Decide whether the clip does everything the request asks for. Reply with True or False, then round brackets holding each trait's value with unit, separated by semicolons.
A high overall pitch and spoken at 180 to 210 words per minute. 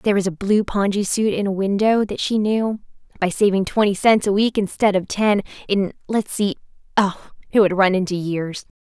True (200 Hz; 185 wpm)